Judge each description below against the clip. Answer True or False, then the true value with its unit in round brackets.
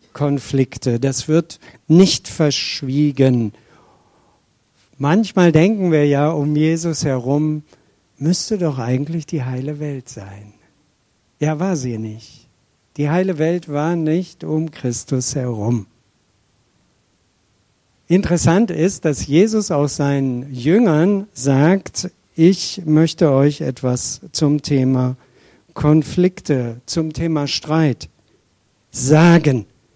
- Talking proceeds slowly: True (100 wpm)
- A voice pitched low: False (145 Hz)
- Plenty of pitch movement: False (4.4 semitones)